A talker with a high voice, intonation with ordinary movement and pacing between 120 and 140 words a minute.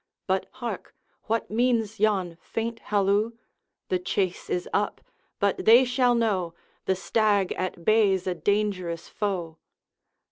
Yes: high, 205 Hz; average, 3.3 semitones; slow, 135 wpm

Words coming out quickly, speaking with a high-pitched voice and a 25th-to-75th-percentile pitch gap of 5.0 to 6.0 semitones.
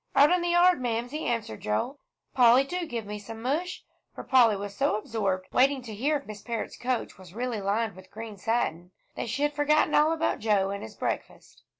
Yes: fast, 210 wpm; high, 235 Hz; wide, 5.5 semitones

